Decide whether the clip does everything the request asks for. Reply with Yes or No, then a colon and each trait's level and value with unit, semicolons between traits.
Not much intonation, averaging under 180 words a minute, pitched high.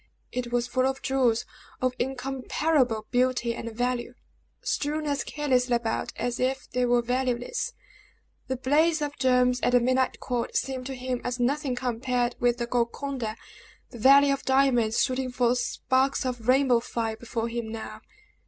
Yes: narrow, 1.8 semitones; average, 160 wpm; very high, 250 Hz